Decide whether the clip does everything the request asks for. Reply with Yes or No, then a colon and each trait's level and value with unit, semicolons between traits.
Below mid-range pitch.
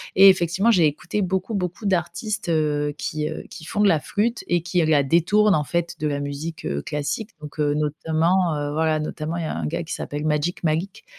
No: medium, 165 Hz